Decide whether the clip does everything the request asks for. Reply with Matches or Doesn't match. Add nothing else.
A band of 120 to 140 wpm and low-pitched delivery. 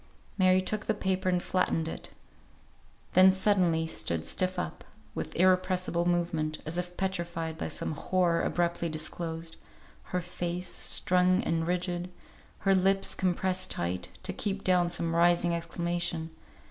Doesn't match